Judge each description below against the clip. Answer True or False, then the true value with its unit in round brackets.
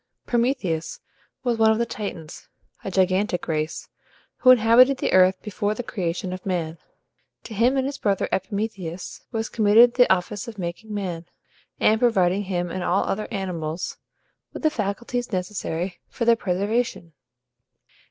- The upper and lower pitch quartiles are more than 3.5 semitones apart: True (4.3 semitones)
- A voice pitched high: True (200 Hz)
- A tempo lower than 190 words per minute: True (150 wpm)